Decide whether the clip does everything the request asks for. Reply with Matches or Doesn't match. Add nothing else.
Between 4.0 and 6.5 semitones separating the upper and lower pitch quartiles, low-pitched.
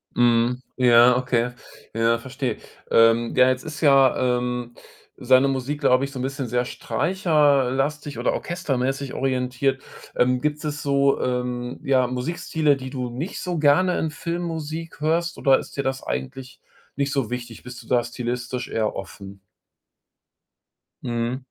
Doesn't match